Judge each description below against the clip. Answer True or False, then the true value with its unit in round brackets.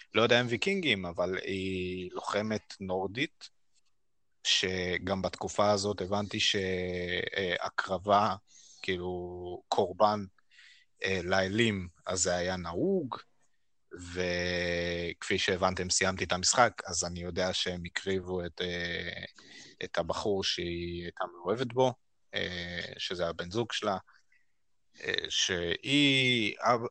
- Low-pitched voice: True (95 Hz)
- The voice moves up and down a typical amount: True (3.8 semitones)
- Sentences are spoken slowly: True (95 wpm)